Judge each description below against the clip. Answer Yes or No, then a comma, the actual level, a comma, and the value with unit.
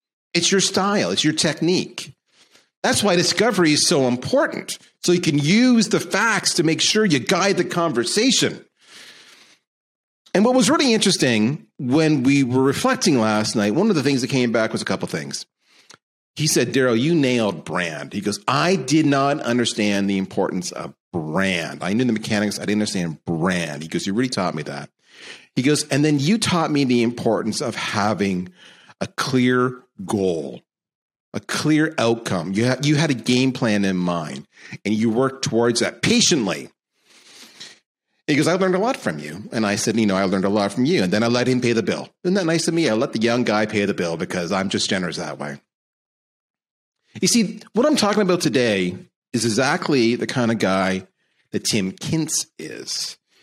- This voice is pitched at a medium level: No, low, 130 Hz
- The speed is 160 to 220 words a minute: Yes, average, 195 wpm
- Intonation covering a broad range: Yes, wide, 8.2 semitones